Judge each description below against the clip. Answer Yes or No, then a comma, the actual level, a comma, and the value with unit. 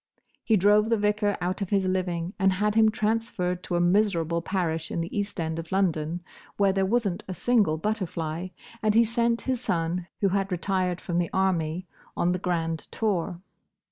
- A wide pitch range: No, average, 3.4 semitones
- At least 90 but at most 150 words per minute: No, average, 190 wpm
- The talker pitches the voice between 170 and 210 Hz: Yes, medium, 185 Hz